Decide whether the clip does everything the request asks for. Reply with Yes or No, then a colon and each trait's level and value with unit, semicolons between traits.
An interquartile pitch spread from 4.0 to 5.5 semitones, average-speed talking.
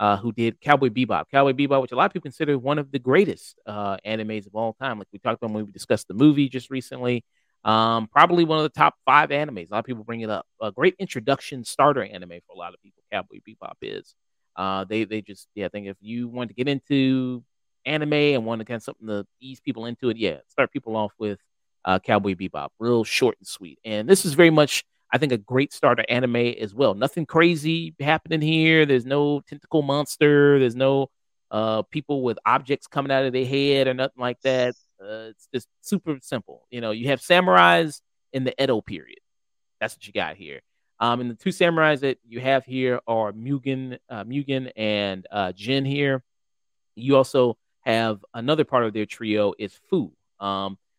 No: average, 4.3 semitones; fast, 210 wpm